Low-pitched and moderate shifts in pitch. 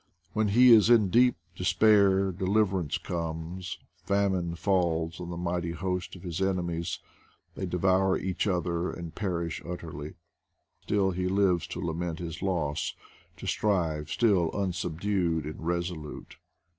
No: very low, 90 Hz; narrow, 2.3 semitones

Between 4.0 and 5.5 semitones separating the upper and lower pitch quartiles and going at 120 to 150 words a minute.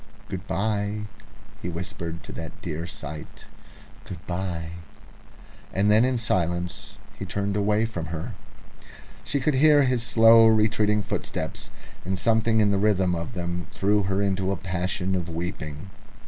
No: average, 3.6 semitones; average, 145 wpm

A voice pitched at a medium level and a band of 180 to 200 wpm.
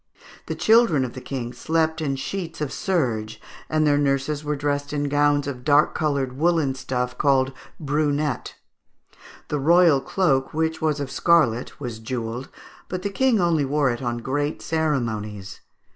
No: medium, 145 Hz; average, 160 wpm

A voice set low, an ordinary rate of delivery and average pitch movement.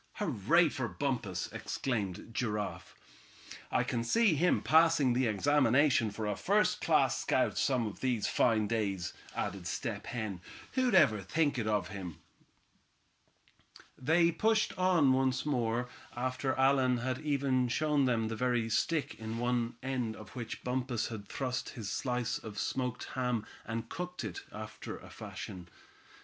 Yes: low, 125 Hz; average, 145 wpm; average, 3.9 semitones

